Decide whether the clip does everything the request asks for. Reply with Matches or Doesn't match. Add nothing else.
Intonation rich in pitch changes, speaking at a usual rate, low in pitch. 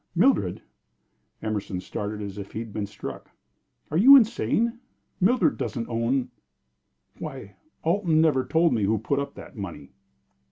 Matches